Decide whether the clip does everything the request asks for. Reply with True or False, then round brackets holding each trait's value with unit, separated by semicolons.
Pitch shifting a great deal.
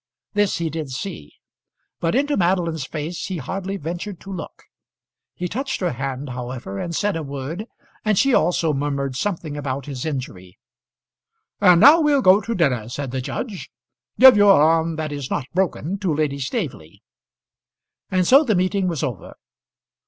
True (6.0 semitones)